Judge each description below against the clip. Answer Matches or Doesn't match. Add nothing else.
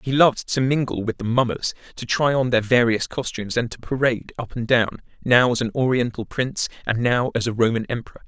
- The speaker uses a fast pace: Matches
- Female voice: Doesn't match